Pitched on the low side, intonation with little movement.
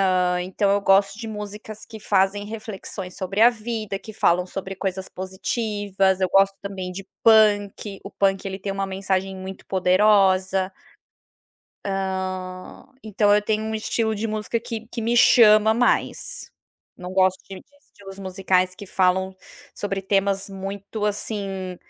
No: high, 195 Hz; narrow, 2.0 semitones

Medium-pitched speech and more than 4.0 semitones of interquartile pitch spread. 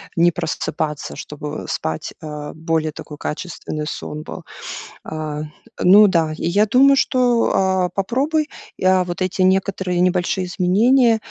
Yes: medium, 180 Hz; average, 4.6 semitones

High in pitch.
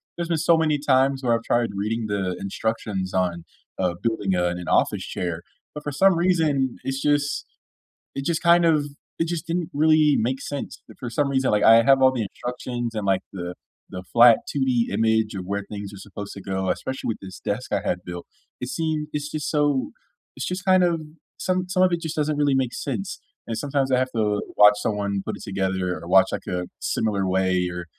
No: low, 120 Hz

